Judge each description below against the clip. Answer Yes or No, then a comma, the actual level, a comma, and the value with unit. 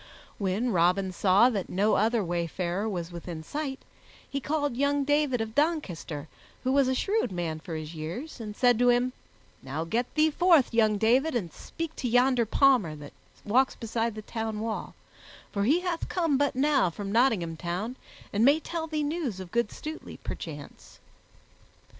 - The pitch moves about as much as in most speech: No, wide, 7.2 semitones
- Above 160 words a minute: Yes, average, 170 wpm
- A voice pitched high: Yes, high, 230 Hz